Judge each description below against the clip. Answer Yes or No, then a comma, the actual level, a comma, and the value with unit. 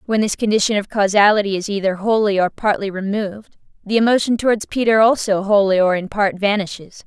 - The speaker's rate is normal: Yes, average, 180 wpm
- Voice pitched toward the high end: Yes, high, 205 Hz